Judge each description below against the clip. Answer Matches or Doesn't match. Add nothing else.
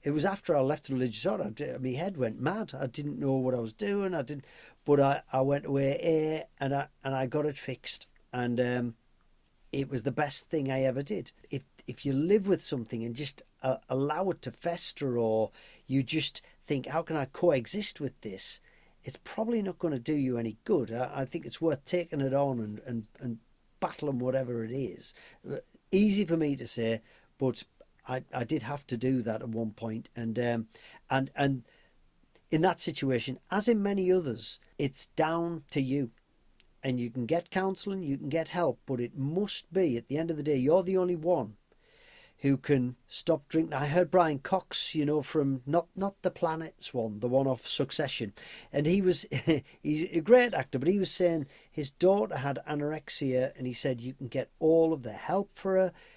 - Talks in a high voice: Doesn't match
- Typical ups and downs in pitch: Matches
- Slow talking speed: Doesn't match